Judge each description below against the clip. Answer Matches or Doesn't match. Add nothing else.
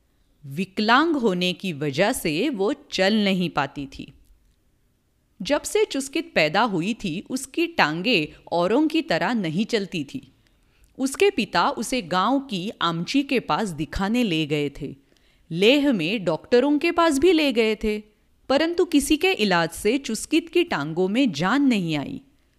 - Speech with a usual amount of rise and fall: Doesn't match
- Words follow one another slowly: Doesn't match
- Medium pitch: Doesn't match